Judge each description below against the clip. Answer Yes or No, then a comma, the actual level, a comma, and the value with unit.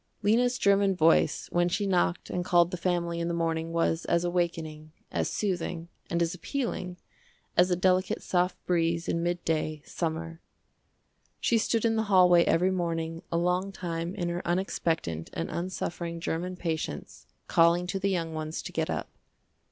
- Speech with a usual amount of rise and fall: No, narrow, 1.7 semitones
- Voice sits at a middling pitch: Yes, medium, 175 Hz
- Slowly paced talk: No, average, 165 wpm